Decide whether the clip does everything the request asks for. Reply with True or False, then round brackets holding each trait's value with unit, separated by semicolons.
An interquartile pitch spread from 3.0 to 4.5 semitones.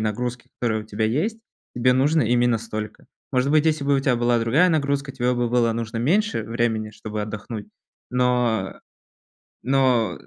True (3.3 semitones)